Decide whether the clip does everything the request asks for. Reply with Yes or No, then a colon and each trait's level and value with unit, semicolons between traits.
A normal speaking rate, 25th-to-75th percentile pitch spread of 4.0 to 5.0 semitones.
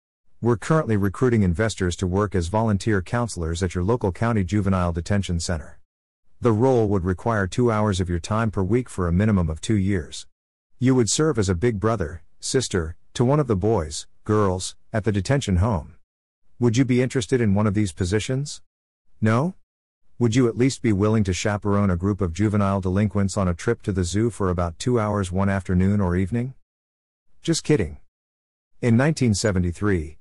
Yes: average, 185 wpm; average, 4.5 semitones